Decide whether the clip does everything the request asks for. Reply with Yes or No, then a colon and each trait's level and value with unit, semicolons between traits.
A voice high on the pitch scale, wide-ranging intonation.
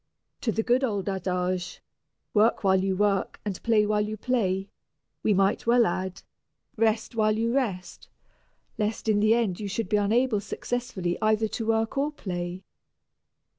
No: high, 210 Hz; average, 3.0 semitones